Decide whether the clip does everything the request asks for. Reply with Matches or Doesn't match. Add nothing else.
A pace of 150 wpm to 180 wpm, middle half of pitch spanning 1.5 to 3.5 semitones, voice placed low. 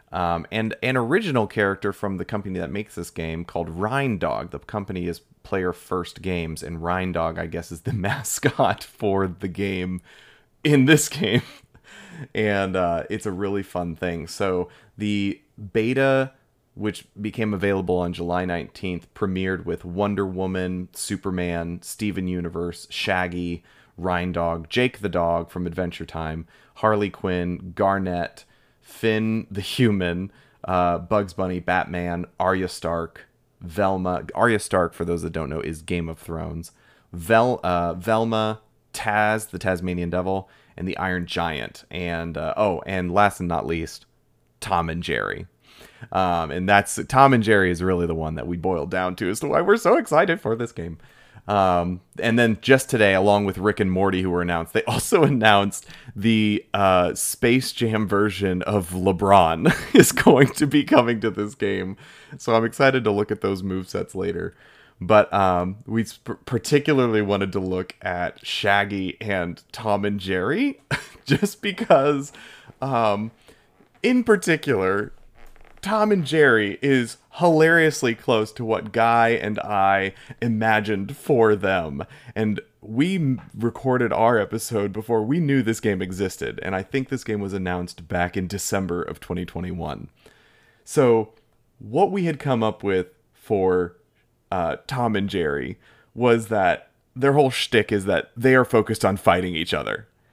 Doesn't match